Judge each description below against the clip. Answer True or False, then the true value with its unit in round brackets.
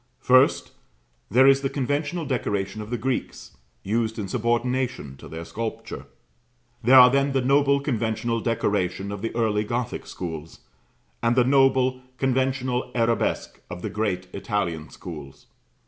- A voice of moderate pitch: False (120 Hz)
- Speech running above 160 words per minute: False (140 wpm)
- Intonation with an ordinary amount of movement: True (4.1 semitones)